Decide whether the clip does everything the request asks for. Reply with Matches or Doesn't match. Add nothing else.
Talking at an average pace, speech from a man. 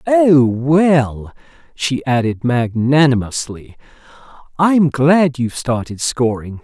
Doesn't match